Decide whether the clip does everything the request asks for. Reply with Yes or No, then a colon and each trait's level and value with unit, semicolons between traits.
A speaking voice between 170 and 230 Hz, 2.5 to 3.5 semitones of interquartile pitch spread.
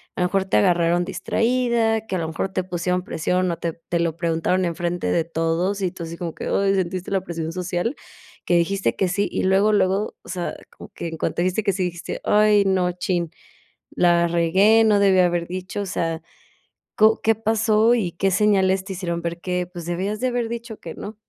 Yes: medium, 185 Hz; average, 2.9 semitones